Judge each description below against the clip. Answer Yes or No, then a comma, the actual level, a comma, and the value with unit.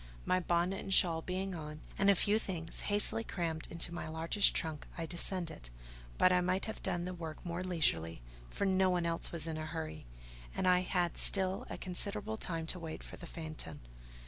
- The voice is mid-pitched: Yes, medium, 175 Hz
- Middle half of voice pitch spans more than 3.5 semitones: No, narrow, 2.5 semitones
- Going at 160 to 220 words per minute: Yes, average, 200 wpm